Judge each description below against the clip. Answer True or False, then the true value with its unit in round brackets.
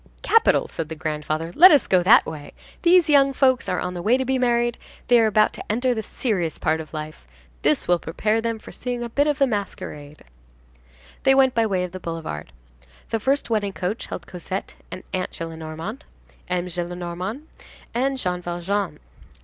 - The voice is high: True (200 Hz)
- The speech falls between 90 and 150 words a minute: False (190 wpm)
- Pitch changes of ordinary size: False (6.2 semitones)